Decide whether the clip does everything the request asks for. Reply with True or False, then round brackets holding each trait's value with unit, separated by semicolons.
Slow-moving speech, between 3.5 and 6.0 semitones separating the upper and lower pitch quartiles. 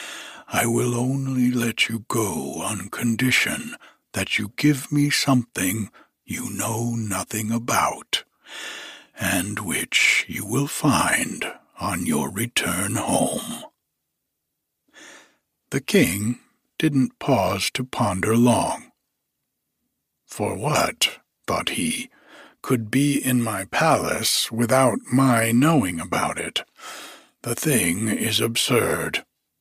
False (105 wpm; 2.9 semitones)